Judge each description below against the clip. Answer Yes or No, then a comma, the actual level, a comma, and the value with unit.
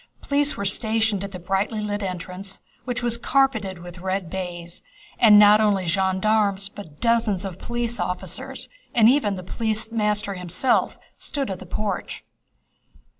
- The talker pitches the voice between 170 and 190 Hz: No, high, 205 Hz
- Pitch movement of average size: Yes, average, 3.0 semitones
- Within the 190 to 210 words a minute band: No, average, 150 wpm